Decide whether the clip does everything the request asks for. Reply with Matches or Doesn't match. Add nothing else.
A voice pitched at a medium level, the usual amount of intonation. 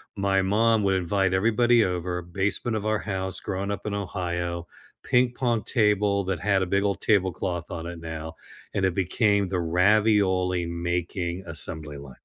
Doesn't match